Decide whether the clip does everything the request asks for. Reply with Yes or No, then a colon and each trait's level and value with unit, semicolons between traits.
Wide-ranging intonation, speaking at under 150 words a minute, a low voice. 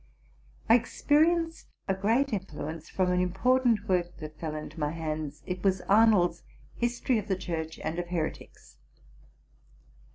No: wide, 5.7 semitones; average, 140 wpm; medium, 185 Hz